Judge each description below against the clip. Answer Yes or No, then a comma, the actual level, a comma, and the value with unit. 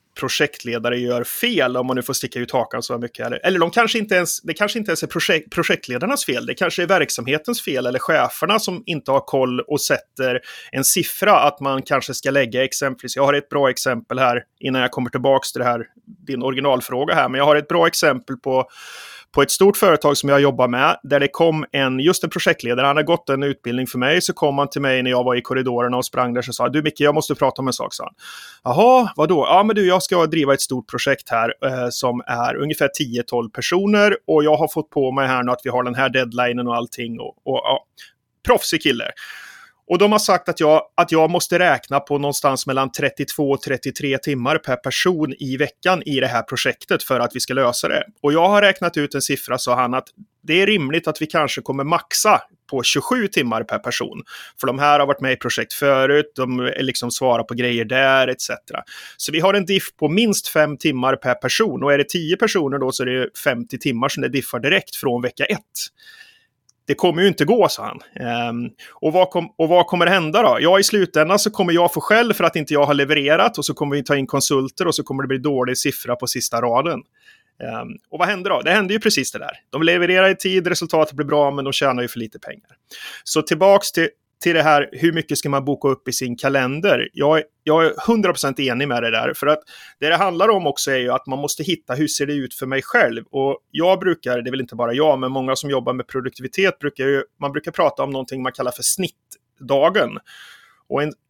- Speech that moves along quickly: Yes, fast, 235 wpm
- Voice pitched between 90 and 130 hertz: No, medium, 140 Hz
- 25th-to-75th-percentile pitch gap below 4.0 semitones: No, average, 4.8 semitones